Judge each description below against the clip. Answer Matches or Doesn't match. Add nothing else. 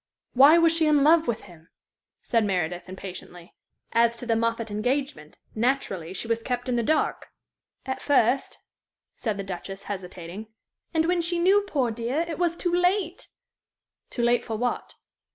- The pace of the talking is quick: Doesn't match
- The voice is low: Doesn't match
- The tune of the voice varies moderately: Doesn't match